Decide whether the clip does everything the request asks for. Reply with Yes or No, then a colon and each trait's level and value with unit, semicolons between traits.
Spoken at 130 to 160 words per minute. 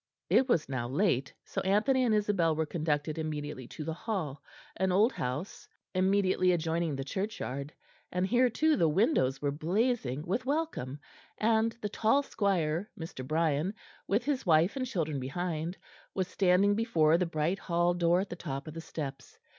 No: average, 170 wpm